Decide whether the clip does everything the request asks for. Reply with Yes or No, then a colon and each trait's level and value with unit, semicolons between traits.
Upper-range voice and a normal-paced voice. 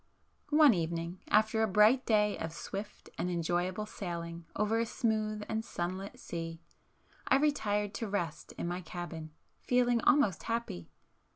Yes: high, 205 Hz; average, 145 wpm